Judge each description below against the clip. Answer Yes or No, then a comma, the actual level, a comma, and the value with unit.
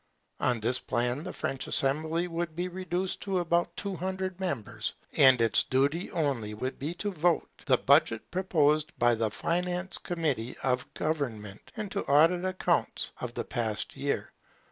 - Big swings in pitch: Yes, wide, 6.2 semitones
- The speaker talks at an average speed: Yes, average, 165 wpm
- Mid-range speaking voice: Yes, medium, 155 Hz